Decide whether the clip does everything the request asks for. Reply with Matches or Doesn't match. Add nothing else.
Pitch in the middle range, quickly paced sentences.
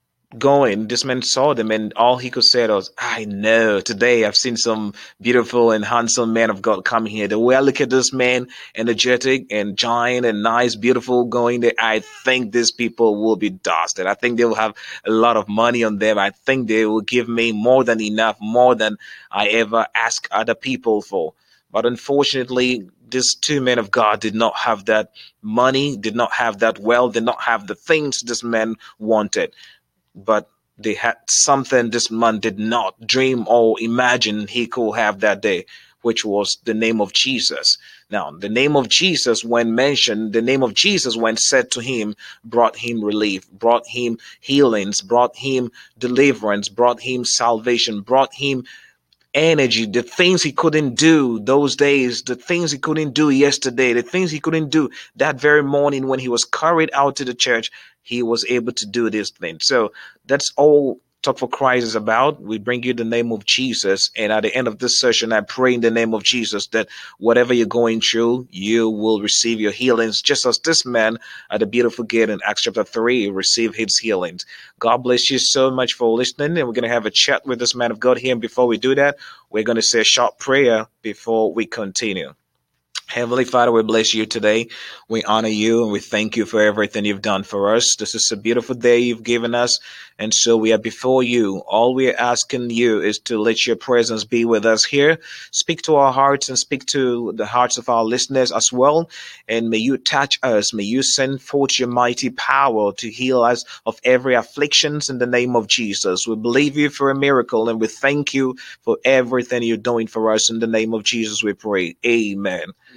Doesn't match